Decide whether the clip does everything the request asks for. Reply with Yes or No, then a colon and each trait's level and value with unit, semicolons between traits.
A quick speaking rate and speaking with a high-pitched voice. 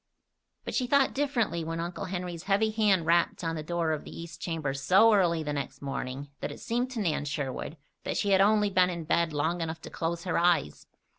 No: fast, 220 wpm; medium, 170 Hz